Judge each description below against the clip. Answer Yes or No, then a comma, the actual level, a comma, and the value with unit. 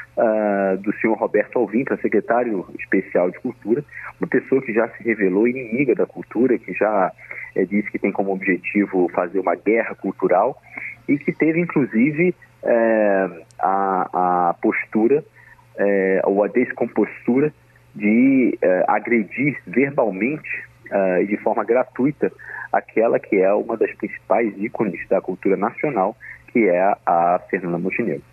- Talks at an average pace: Yes, average, 145 wpm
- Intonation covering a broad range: Yes, wide, 7.1 semitones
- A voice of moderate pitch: No, low, 105 Hz